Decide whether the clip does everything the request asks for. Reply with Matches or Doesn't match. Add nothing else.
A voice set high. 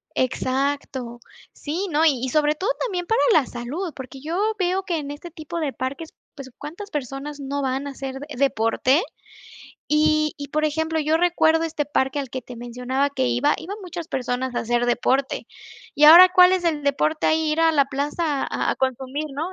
Matches